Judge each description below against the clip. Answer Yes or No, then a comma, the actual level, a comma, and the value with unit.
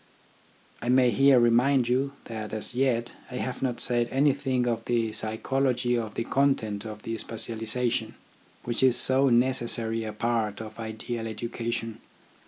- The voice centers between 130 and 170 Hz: No, low, 120 Hz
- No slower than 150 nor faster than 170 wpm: Yes, average, 155 wpm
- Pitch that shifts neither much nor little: No, narrow, 2.3 semitones